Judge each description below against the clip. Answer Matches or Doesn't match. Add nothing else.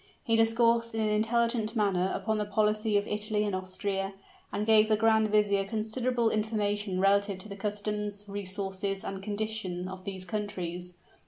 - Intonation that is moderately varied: Doesn't match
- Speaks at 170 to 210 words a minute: Doesn't match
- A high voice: Matches